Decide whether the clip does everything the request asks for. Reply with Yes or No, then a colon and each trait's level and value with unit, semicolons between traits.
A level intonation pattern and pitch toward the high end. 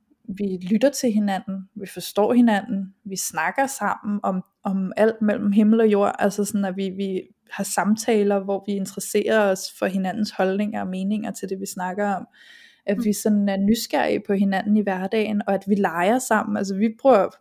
Yes: narrow, 1.9 semitones; high, 205 Hz